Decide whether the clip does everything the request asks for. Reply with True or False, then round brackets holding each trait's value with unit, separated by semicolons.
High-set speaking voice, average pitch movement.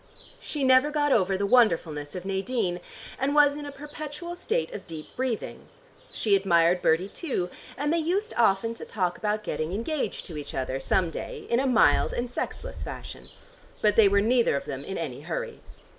False (220 Hz; 8.2 semitones)